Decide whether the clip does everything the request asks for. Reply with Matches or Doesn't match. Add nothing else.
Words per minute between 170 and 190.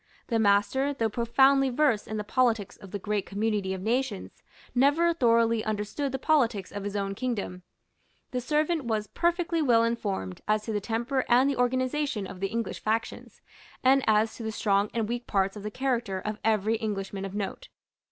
Matches